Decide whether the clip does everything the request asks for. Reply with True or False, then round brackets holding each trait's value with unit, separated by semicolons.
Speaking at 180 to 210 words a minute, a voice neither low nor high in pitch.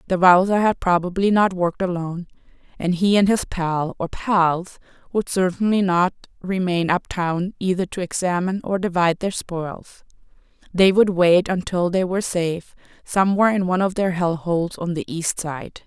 False (165 wpm; 180 Hz)